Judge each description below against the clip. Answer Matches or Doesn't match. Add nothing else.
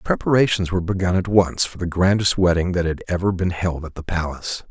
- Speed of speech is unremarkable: Doesn't match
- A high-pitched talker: Doesn't match